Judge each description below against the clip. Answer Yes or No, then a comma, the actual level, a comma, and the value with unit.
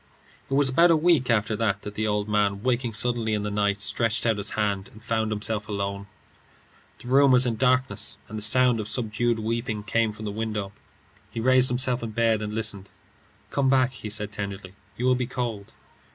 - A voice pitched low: Yes, low, 110 Hz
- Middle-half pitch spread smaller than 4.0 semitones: Yes, average, 3.0 semitones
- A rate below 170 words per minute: No, average, 200 wpm